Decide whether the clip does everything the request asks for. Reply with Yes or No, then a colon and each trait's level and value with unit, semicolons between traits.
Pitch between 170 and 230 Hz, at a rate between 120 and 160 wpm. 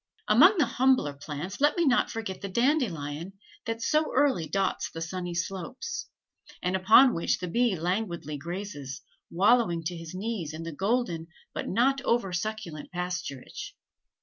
Yes: high, 190 Hz; average, 150 wpm